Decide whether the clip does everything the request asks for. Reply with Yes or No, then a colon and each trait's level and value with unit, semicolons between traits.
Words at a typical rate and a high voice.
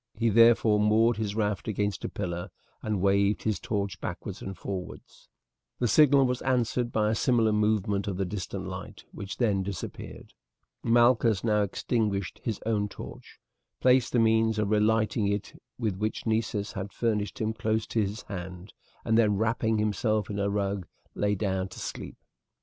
No: average, 165 wpm; low, 105 Hz